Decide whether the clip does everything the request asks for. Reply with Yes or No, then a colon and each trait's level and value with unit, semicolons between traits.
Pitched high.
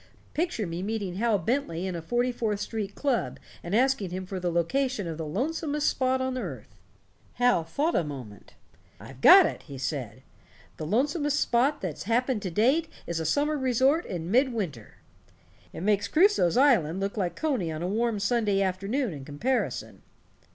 Yes: high, 210 Hz